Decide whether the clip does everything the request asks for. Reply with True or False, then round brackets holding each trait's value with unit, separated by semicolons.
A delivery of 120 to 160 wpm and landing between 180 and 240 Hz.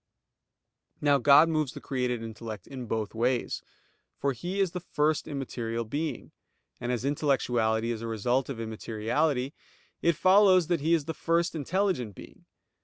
False (155 wpm; 135 Hz)